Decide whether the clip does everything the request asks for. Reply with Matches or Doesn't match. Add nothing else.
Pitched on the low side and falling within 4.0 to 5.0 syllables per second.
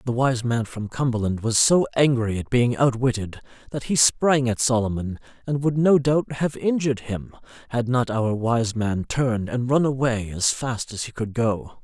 Matches